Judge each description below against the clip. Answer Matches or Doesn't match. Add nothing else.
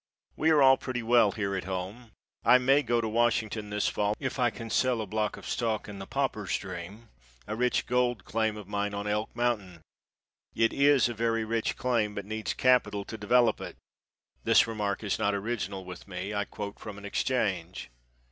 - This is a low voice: Matches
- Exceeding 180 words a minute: Matches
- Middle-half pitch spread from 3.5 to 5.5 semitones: Doesn't match